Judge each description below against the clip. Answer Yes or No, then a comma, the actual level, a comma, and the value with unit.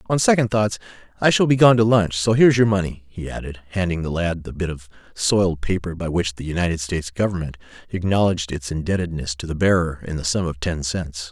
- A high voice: No, very low, 90 Hz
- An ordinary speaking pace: No, fast, 215 wpm